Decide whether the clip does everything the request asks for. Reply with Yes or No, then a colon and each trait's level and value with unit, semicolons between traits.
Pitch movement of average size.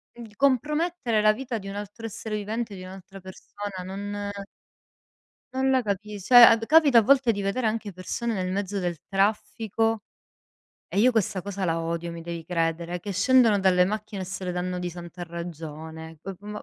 Yes: average, 3.8 semitones